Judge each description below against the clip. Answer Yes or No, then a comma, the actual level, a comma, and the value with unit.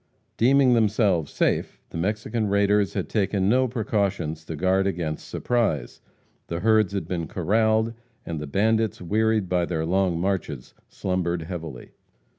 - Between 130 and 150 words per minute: Yes, average, 140 wpm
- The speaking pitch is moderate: No, very low, 95 Hz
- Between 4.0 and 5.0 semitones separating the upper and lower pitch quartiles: Yes, average, 4.5 semitones